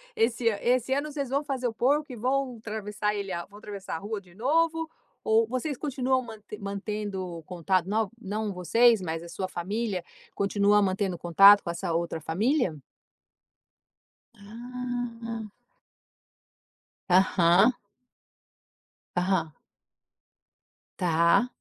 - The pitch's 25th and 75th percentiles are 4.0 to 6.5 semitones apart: Yes, average, 4.6 semitones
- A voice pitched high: Yes, high, 210 Hz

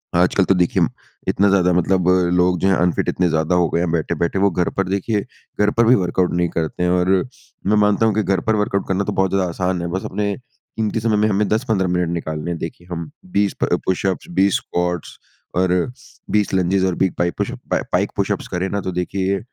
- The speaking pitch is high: No, very low, 95 Hz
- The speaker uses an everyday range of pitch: No, narrow, 2.1 semitones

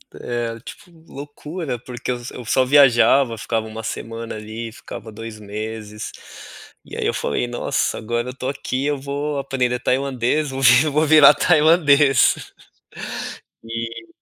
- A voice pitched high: No, low, 125 Hz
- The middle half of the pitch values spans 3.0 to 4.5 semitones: Yes, average, 3.7 semitones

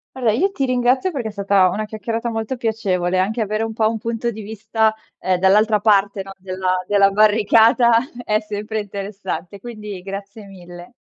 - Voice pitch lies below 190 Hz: No, high, 215 Hz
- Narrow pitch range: Yes, narrow, 2.3 semitones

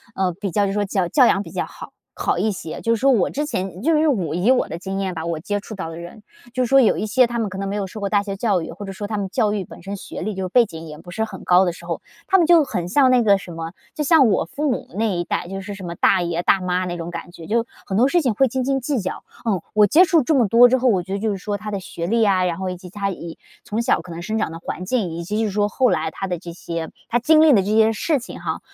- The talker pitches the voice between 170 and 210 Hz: Yes, high, 200 Hz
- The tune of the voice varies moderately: Yes, average, 4.6 semitones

